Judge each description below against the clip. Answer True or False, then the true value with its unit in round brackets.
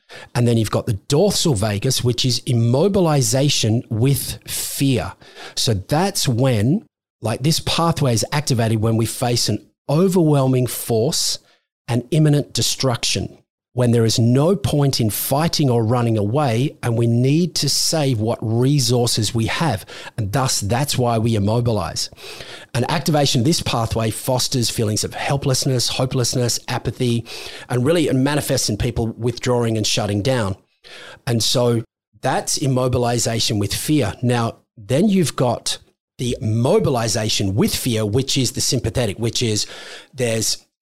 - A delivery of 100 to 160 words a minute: True (140 wpm)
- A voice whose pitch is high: False (120 Hz)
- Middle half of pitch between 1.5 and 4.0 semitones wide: True (3.1 semitones)